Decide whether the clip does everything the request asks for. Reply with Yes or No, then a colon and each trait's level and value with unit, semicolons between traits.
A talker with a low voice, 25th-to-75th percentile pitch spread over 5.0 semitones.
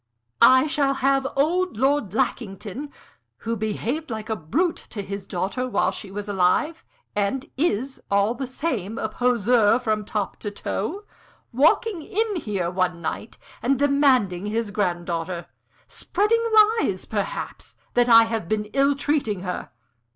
No: high, 230 Hz; wide, 5.6 semitones